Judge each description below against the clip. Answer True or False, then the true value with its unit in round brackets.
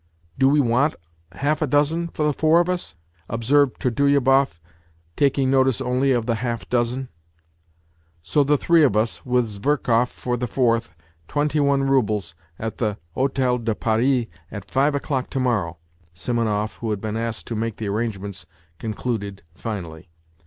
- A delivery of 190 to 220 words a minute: False (170 wpm)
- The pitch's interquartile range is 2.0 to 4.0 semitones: False (4.4 semitones)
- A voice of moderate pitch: False (120 Hz)